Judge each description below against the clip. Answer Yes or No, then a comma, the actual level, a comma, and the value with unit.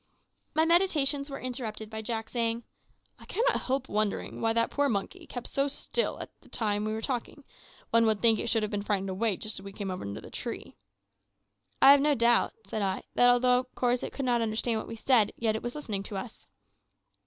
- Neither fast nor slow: No, fast, 220 wpm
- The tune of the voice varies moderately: Yes, average, 3.4 semitones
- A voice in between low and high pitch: No, high, 230 Hz